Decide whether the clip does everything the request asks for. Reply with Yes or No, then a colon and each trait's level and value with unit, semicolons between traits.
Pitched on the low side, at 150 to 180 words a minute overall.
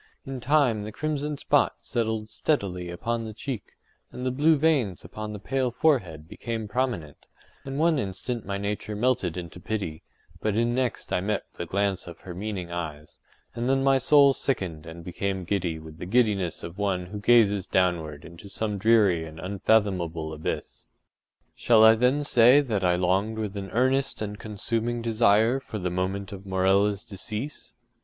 Yes: low, 105 Hz; average, 170 wpm